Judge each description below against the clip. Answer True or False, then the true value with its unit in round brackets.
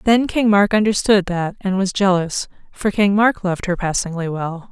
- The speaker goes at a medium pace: True (190 wpm)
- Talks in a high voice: True (195 Hz)